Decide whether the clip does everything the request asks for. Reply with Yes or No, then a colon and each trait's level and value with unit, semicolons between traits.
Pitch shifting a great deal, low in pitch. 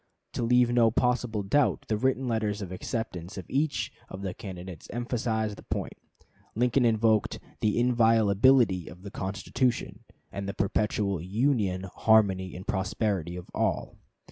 No: average, 4.0 semitones; low, 105 Hz